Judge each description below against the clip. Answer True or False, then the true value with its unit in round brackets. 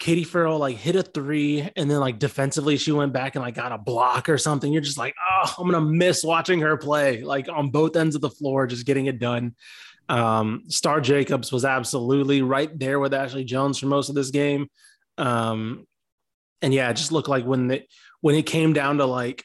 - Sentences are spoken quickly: True (220 wpm)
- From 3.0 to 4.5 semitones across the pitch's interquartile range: False (2.6 semitones)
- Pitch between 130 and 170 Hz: True (140 Hz)